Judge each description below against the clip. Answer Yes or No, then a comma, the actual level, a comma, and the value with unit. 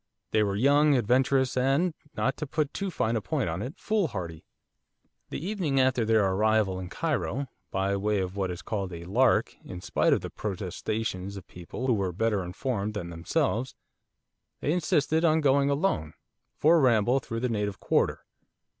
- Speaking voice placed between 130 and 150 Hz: No, low, 115 Hz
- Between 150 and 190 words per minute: Yes, average, 175 wpm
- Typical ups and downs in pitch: No, wide, 6.2 semitones